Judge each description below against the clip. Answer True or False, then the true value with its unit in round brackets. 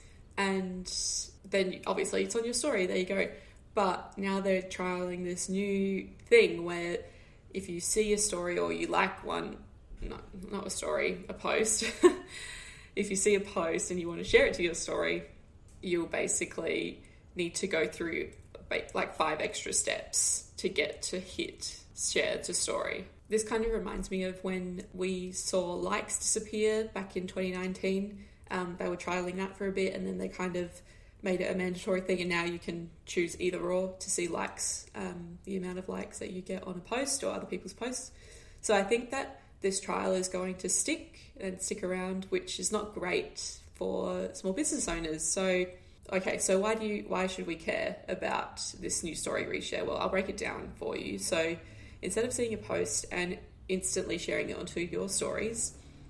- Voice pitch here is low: False (185 Hz)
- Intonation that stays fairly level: True (2.2 semitones)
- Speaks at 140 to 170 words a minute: False (190 wpm)